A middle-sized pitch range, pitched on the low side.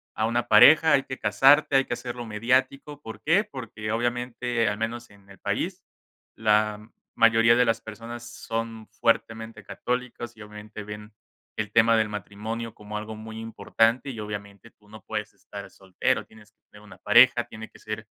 No: narrow, 2.1 semitones; low, 115 Hz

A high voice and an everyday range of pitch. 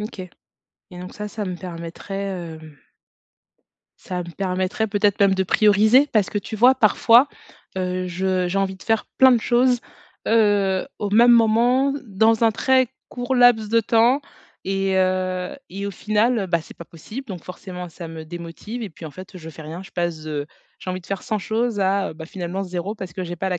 Yes: high, 195 Hz; average, 3.6 semitones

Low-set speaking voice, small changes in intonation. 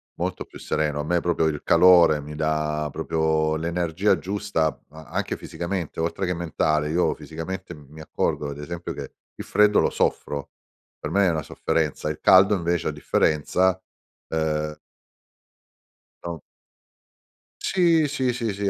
No: very low, 80 Hz; average, 3.4 semitones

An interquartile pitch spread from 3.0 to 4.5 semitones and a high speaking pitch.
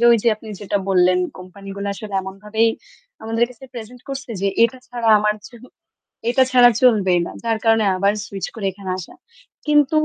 Yes: average, 3.3 semitones; high, 220 Hz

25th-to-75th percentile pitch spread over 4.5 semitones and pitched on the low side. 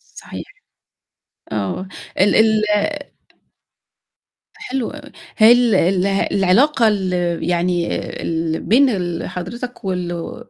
No: average, 5.2 semitones; high, 195 Hz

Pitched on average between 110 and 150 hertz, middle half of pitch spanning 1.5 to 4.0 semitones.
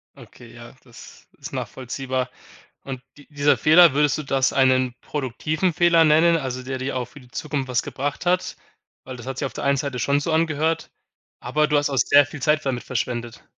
Yes: medium, 140 Hz; average, 2.9 semitones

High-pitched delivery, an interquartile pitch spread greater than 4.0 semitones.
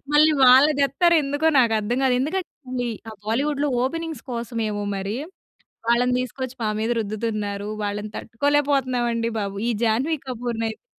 Yes: high, 245 Hz; average, 4.4 semitones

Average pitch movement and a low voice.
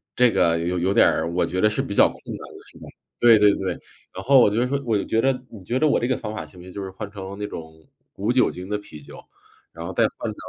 Yes: average, 4.4 semitones; low, 100 Hz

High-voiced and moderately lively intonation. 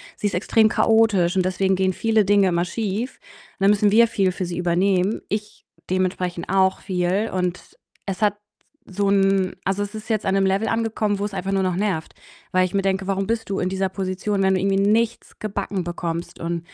No: high, 195 Hz; narrow, 2.0 semitones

